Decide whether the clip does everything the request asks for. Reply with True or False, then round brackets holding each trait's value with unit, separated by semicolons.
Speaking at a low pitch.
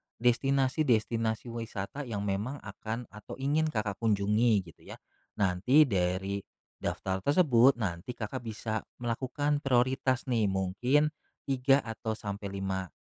True (115 Hz)